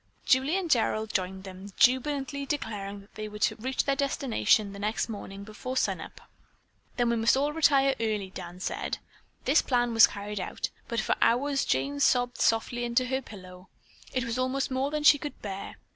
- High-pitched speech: Yes, high, 235 Hz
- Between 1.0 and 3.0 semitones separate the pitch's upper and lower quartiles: No, average, 4.9 semitones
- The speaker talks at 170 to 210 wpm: Yes, average, 190 wpm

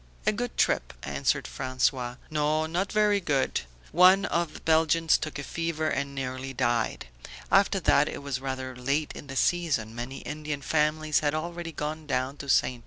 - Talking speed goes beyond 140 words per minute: Yes, average, 175 wpm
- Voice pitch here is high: No, medium, 150 Hz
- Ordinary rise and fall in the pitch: Yes, average, 3.6 semitones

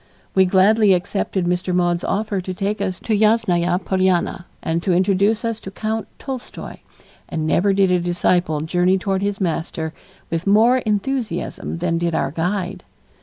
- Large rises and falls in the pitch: No, average, 2.8 semitones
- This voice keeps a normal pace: Yes, average, 160 wpm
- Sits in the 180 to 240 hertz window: Yes, high, 190 Hz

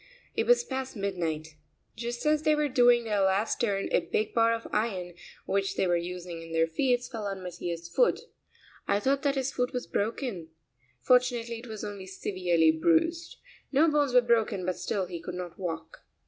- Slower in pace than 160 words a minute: No, average, 190 wpm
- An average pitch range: No, wide, 5.8 semitones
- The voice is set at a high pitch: Yes, high, 210 Hz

